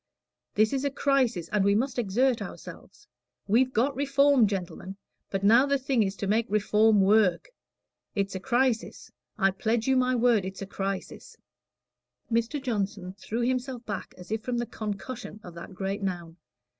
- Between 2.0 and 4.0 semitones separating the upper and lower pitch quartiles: No, average, 4.4 semitones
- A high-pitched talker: Yes, high, 220 Hz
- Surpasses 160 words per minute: Yes, average, 170 wpm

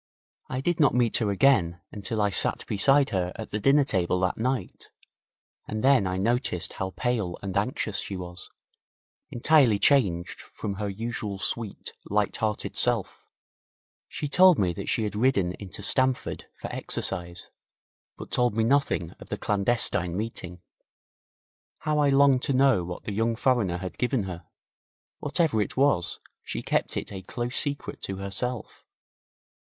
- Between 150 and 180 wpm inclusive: Yes, average, 155 wpm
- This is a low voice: Yes, low, 110 Hz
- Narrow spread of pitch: No, average, 5.3 semitones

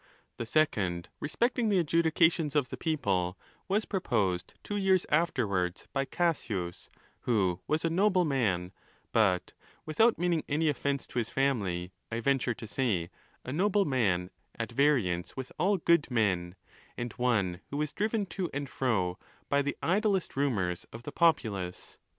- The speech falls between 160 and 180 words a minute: No, average, 150 wpm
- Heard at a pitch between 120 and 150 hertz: Yes, low, 135 Hz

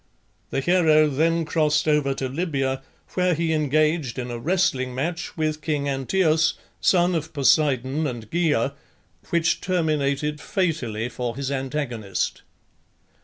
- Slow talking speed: Yes, slow, 125 wpm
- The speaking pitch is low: No, medium, 150 Hz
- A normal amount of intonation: Yes, average, 3.5 semitones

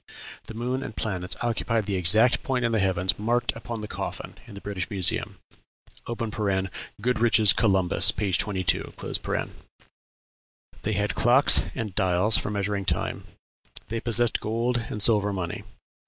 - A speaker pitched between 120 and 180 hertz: No, low, 105 Hz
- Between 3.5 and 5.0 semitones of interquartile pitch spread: No, average, 3.1 semitones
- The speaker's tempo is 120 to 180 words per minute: Yes, average, 140 wpm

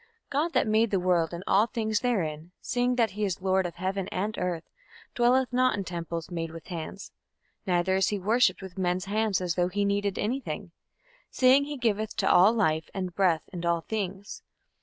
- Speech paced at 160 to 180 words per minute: No, average, 195 wpm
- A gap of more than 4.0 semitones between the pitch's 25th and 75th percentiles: No, average, 3.7 semitones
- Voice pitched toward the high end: Yes, high, 195 Hz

